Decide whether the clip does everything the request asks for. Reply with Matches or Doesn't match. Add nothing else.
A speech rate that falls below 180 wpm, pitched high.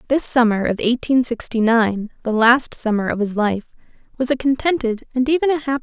Doesn't match